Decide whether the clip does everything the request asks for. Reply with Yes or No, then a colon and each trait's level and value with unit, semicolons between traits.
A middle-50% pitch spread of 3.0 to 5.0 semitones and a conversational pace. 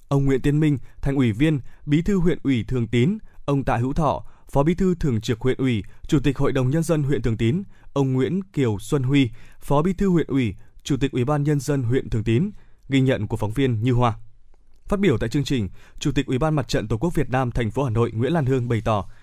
No: average, 3.9 semitones; fast, 260 wpm